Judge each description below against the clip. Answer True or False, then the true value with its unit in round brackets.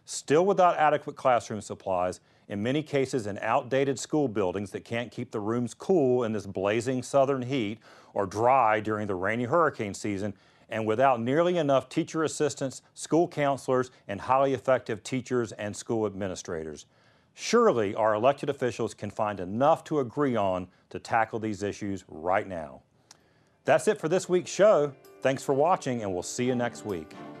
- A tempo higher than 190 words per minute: False (165 wpm)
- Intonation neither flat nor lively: True (4.9 semitones)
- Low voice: True (125 Hz)